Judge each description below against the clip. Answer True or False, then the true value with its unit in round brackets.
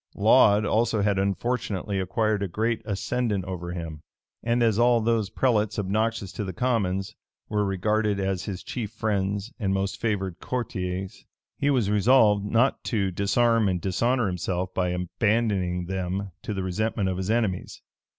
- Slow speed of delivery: False (155 wpm)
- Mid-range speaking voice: False (100 Hz)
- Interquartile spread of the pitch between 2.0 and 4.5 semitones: True (3.2 semitones)